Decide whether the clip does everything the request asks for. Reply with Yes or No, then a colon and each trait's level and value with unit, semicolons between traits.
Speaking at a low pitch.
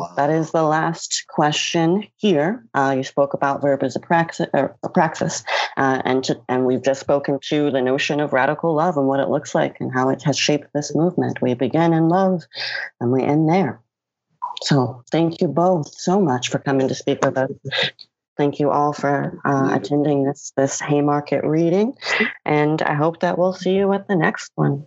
No: medium, 145 Hz